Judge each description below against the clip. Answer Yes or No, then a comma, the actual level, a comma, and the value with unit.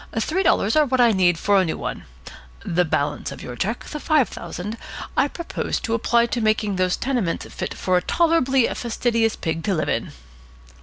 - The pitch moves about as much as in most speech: No, wide, 5.8 semitones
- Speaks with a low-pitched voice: No, high, 220 Hz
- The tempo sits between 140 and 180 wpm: No, average, 195 wpm